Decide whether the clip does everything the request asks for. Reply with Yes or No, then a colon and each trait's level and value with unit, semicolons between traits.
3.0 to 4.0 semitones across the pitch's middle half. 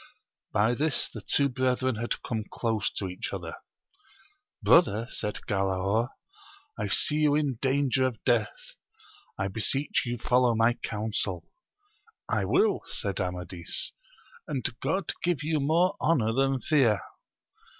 No: average, 5.0 semitones